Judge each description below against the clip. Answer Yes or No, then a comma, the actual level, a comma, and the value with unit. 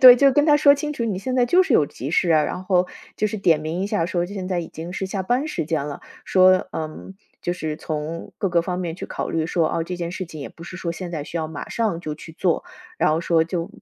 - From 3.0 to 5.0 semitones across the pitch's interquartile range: Yes, average, 3.4 semitones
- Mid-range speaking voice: Yes, medium, 175 Hz